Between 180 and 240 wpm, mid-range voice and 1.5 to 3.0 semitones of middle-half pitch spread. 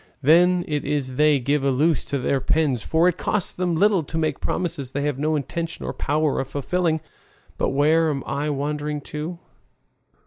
Yes: average, 185 wpm; medium, 150 Hz; average, 2.7 semitones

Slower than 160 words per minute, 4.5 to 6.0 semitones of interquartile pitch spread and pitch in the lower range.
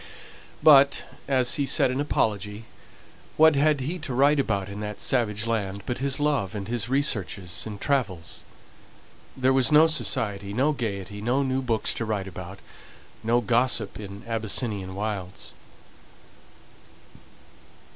Yes: slow, 135 wpm; average, 4.9 semitones; low, 115 Hz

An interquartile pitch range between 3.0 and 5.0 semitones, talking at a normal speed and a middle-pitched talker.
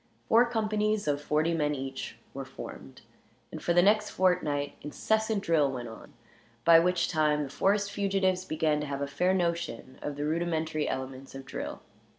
Yes: average, 4.7 semitones; average, 170 wpm; medium, 160 Hz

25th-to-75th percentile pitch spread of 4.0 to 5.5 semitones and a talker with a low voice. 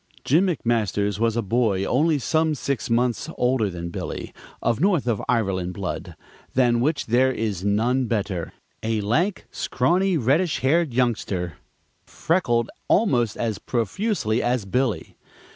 Yes: average, 4.7 semitones; low, 120 Hz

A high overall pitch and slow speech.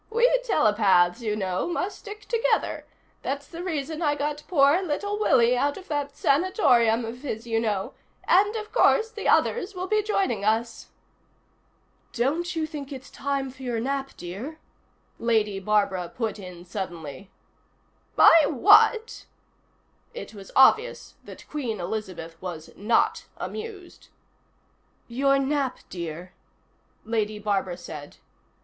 Yes: very high, 265 Hz; slow, 130 wpm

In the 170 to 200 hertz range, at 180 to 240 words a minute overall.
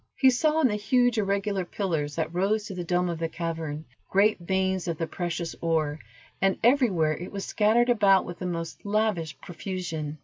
Yes: medium, 185 Hz; average, 190 wpm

